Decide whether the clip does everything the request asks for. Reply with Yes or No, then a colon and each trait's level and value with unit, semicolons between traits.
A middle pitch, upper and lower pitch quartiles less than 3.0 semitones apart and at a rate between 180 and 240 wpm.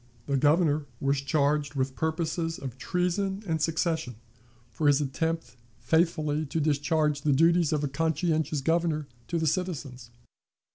No: medium, 155 Hz; narrow, 2.5 semitones; average, 140 wpm